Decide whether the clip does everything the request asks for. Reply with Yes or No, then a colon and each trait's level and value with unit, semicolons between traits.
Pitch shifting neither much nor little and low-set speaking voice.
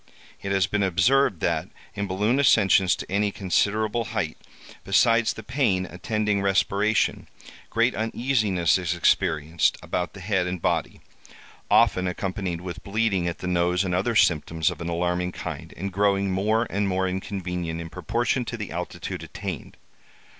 Yes: average, 3.2 semitones; very low, 95 Hz